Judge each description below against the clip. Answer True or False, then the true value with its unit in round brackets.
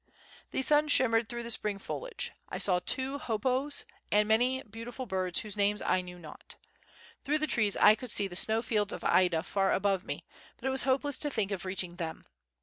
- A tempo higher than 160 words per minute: True (205 wpm)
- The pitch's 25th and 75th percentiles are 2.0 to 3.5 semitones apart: False (5.1 semitones)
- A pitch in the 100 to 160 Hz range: False (220 Hz)